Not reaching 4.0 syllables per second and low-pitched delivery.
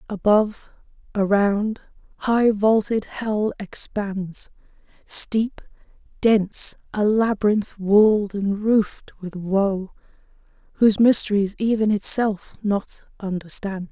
No: 3.6 syllables/s; high, 205 Hz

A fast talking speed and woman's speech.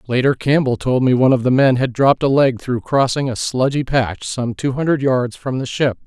No: fast, 240 wpm; male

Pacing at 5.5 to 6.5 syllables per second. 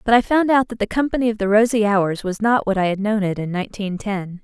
Yes: 6.0 syllables/s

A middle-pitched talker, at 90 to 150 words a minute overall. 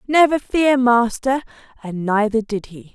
No: high, 240 Hz; average, 140 wpm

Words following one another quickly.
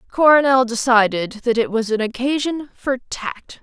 No: average, 150 wpm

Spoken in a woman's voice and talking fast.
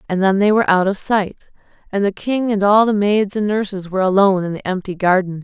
Yes: female; fast, 245 wpm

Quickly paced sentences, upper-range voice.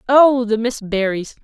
No: average, 165 wpm; high, 230 Hz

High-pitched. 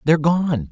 No: medium, 150 Hz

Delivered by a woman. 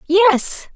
Yes: female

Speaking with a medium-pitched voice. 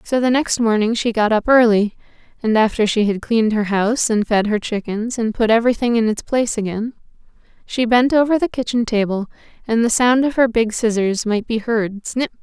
No: high, 225 Hz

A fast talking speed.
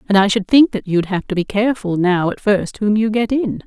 Yes: fast, 280 wpm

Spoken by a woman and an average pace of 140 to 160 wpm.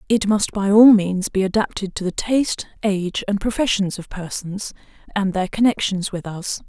No: female; average, 180 wpm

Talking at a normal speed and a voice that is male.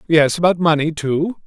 Yes: average, 165 wpm; male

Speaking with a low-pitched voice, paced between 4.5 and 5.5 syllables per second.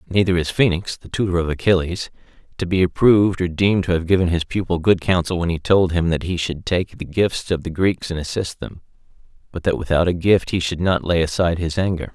No: very low, 90 Hz; 5.8 syllables/s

